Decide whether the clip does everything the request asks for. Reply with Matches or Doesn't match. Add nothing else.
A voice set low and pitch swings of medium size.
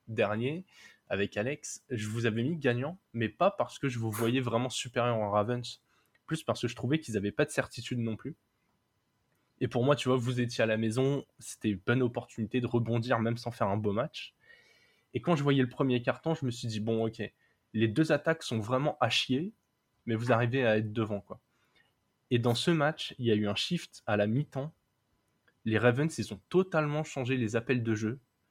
Matches